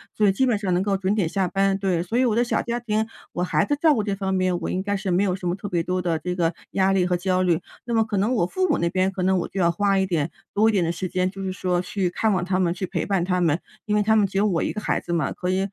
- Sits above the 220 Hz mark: No, high, 190 Hz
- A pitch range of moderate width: No, narrow, 2.3 semitones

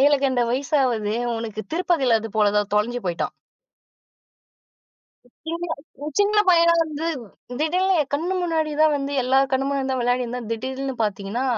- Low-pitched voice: No, very high, 265 Hz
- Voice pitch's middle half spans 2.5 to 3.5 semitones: No, average, 5.3 semitones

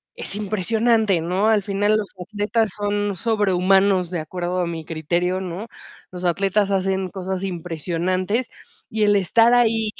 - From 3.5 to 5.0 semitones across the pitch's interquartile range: No, average, 2.8 semitones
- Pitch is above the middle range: Yes, high, 195 Hz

